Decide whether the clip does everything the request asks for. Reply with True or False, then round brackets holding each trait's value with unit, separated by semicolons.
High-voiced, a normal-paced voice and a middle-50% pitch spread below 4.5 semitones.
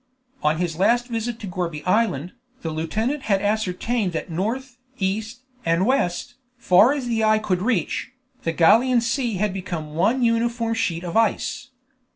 False (215 Hz; 160 wpm; 4.9 semitones)